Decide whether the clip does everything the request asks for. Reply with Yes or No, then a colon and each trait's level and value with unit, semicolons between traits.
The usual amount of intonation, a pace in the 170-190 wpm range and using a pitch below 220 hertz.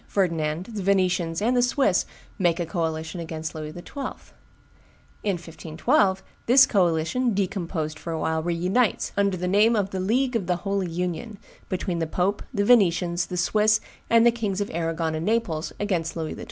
Yes: average, 4.0 semitones; average, 180 wpm; medium, 185 Hz